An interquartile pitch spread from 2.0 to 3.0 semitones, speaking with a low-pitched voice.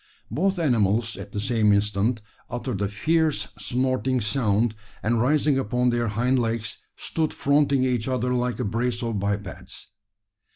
No: average, 3.6 semitones; low, 120 Hz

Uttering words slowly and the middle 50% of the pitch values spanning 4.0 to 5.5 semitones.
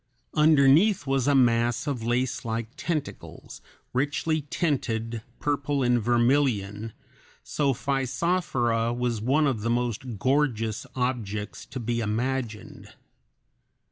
No: slow, 105 wpm; average, 3.4 semitones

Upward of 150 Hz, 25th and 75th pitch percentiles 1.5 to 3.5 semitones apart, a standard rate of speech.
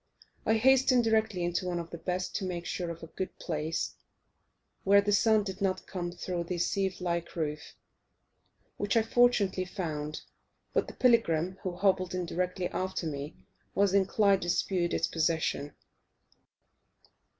Yes: medium, 185 Hz; average, 2.8 semitones; average, 155 wpm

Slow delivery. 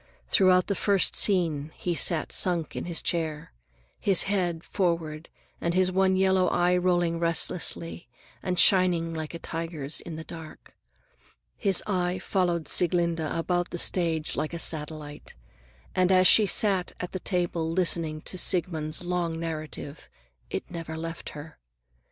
No: average, 145 wpm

